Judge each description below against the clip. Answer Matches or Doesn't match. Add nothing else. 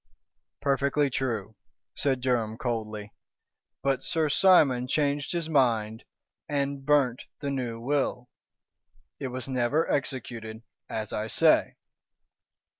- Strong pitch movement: Doesn't match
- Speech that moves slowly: Matches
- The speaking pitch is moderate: Doesn't match